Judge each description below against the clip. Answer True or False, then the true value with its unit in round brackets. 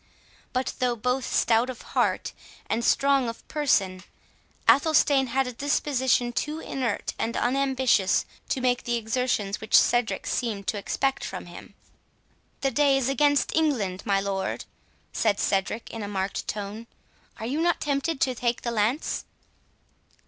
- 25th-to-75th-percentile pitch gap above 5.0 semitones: False (3.7 semitones)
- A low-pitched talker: False (245 Hz)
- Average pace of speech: True (150 wpm)